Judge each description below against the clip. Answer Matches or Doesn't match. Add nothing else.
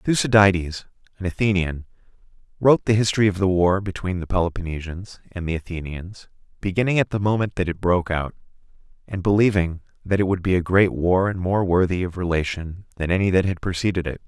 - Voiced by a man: Matches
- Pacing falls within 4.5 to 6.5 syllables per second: Matches